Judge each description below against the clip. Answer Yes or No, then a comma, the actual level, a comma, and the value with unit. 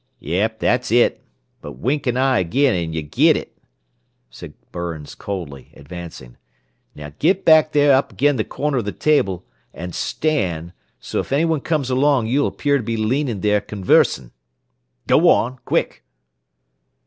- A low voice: Yes, low, 115 Hz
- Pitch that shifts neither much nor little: No, wide, 8.3 semitones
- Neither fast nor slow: Yes, average, 155 wpm